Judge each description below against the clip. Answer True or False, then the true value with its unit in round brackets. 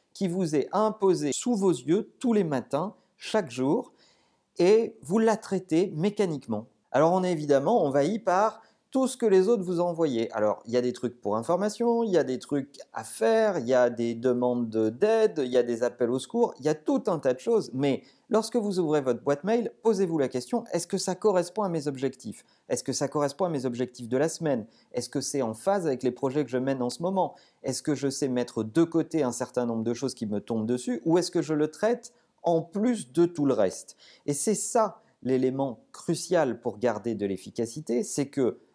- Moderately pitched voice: True (155 Hz)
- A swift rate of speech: True (225 wpm)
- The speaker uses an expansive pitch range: True (8.0 semitones)